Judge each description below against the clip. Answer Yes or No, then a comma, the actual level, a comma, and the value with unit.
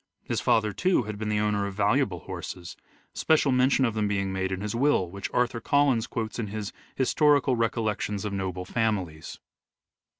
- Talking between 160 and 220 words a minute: Yes, average, 185 wpm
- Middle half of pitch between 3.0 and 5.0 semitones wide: Yes, average, 3.8 semitones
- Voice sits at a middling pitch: No, low, 105 Hz